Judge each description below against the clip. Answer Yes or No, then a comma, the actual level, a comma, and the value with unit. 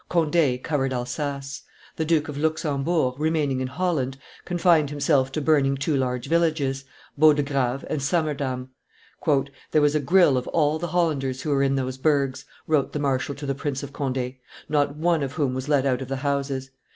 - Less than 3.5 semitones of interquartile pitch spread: Yes, narrow, 2.6 semitones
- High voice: No, medium, 140 Hz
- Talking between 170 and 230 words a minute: Yes, average, 180 wpm